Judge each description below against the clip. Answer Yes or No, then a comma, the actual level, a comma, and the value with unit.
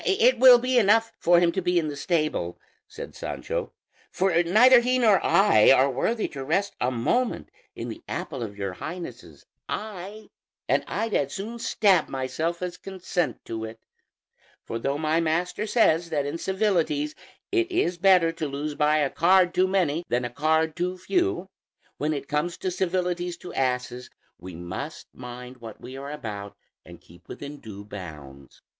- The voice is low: No, medium, 160 Hz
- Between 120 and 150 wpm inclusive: No, average, 175 wpm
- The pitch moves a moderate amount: No, wide, 6.7 semitones